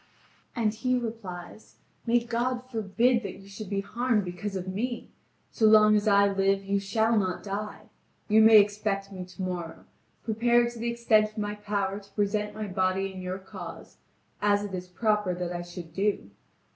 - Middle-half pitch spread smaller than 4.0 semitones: Yes, narrow, 2.4 semitones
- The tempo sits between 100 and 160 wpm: No, average, 180 wpm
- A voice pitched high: Yes, high, 205 Hz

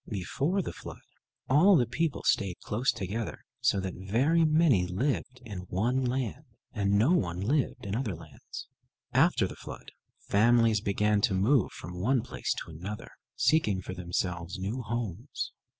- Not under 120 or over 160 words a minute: Yes, average, 155 wpm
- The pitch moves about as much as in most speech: No, wide, 5.7 semitones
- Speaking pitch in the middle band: No, low, 110 Hz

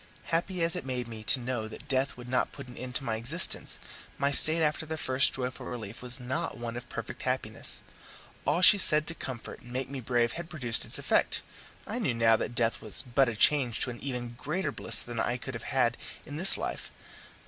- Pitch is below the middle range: Yes, low, 125 Hz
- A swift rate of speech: Yes, fast, 220 wpm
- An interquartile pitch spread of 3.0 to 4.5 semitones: Yes, average, 3.6 semitones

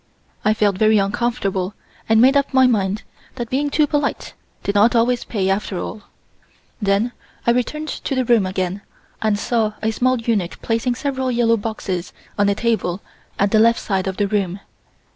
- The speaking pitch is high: Yes, high, 220 Hz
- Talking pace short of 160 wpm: No, average, 180 wpm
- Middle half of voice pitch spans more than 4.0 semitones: No, average, 3.4 semitones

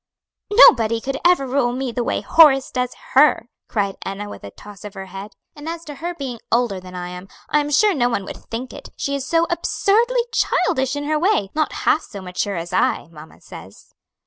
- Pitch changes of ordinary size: No, wide, 7.1 semitones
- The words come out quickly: Yes, fast, 210 wpm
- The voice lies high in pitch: Yes, very high, 250 Hz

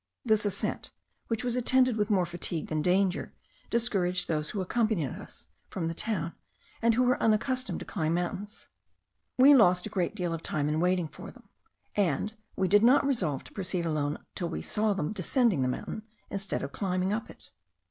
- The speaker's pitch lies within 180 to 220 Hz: Yes, high, 190 Hz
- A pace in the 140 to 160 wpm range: No, average, 190 wpm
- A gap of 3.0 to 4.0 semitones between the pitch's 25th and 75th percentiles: No, average, 4.5 semitones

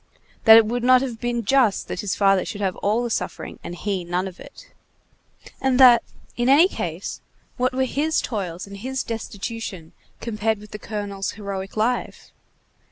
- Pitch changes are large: No, average, 3.9 semitones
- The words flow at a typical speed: Yes, average, 175 wpm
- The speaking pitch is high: Yes, high, 220 Hz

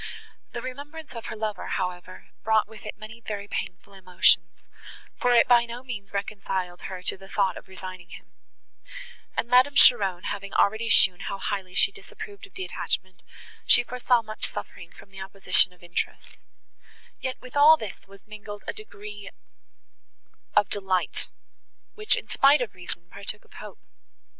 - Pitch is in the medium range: No, high, 205 Hz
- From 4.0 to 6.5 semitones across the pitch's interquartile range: Yes, average, 4.4 semitones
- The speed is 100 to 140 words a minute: No, average, 160 wpm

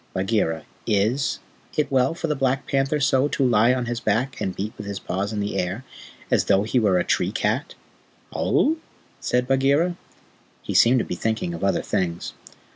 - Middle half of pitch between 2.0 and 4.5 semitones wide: No, average, 5.2 semitones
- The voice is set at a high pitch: No, low, 115 Hz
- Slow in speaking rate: No, average, 190 wpm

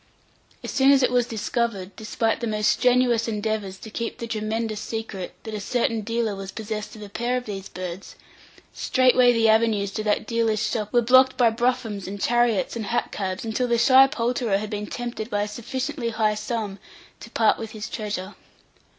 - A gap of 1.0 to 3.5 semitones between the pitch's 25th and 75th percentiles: Yes, narrow, 2.4 semitones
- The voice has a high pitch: Yes, high, 225 Hz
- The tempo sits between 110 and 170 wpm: No, average, 195 wpm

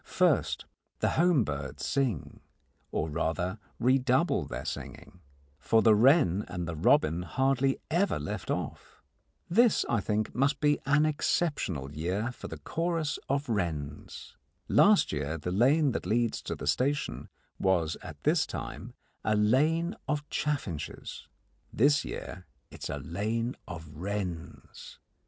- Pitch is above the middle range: No, low, 115 Hz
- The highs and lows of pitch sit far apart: Yes, wide, 8.9 semitones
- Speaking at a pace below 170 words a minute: Yes, average, 140 wpm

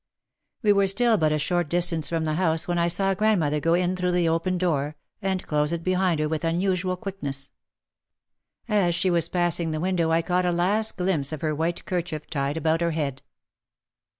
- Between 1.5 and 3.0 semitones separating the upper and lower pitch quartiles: Yes, narrow, 2.6 semitones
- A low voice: No, medium, 170 Hz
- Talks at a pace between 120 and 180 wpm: No, average, 200 wpm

